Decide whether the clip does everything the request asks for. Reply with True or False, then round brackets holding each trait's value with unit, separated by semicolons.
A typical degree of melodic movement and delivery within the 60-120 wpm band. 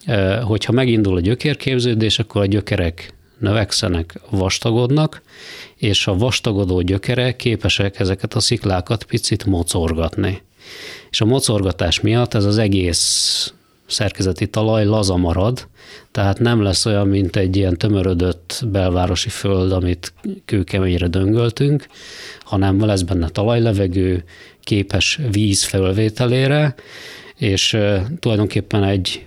True (3.5 semitones; 110 wpm)